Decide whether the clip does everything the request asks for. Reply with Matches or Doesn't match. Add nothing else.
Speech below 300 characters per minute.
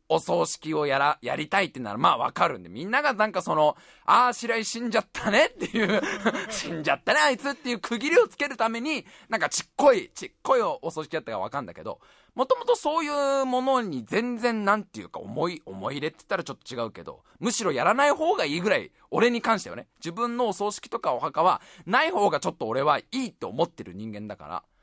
Doesn't match